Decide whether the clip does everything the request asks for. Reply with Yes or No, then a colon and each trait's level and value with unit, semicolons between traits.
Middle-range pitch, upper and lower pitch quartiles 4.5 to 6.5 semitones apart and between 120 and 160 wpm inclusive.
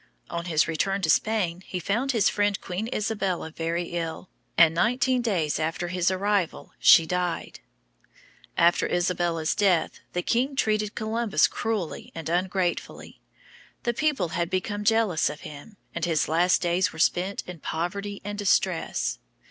No: medium, 180 Hz; average, 3.5 semitones; average, 150 wpm